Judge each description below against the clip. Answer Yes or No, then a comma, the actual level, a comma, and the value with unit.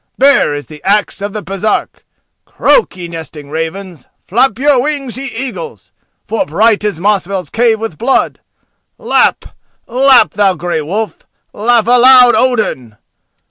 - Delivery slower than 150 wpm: Yes, average, 140 wpm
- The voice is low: No, high, 210 Hz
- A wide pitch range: Yes, wide, 6.0 semitones